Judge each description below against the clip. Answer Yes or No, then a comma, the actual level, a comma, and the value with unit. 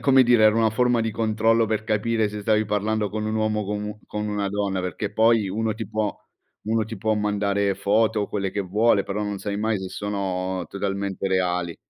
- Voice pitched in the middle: No, low, 105 Hz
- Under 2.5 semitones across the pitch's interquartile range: Yes, narrow, 1.7 semitones